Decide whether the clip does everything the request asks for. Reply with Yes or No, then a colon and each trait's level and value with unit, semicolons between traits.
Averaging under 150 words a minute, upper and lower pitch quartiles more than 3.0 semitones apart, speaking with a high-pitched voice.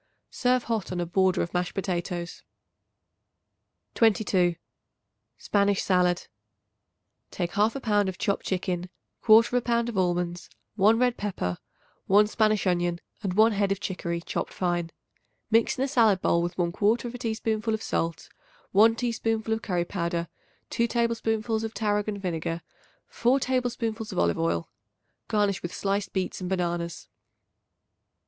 Yes: average, 140 wpm; average, 4.1 semitones; high, 200 Hz